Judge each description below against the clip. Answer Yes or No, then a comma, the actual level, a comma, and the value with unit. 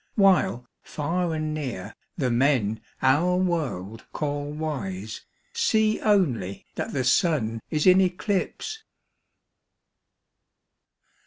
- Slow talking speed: Yes, slow, 95 wpm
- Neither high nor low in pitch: Yes, medium, 150 Hz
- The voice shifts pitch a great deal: Yes, wide, 7.4 semitones